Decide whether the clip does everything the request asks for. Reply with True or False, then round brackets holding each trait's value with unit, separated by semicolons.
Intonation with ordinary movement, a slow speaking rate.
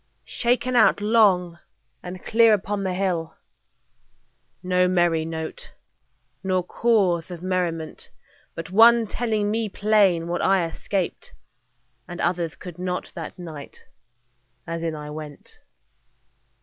True (3.7 semitones; 120 wpm)